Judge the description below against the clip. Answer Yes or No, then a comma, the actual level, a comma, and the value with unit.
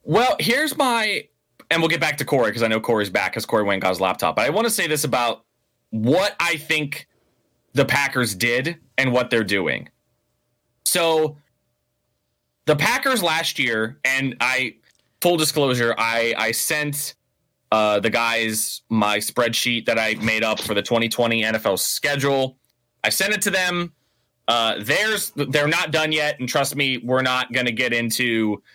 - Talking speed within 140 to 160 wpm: No, average, 175 wpm